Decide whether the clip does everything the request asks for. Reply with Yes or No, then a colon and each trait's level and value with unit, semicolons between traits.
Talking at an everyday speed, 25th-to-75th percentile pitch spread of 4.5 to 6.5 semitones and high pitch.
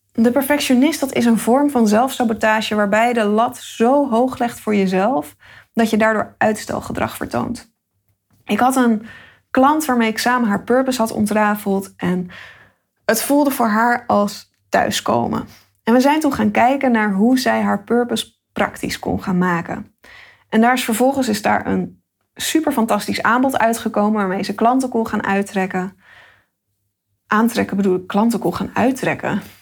No: average, 160 wpm; average, 3.6 semitones; high, 225 Hz